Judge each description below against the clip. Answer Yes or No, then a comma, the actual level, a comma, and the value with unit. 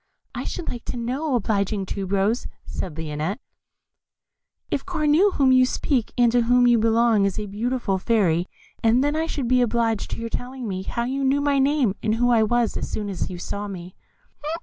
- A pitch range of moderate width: Yes, average, 4.3 semitones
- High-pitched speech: Yes, high, 235 Hz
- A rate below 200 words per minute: No, fast, 205 wpm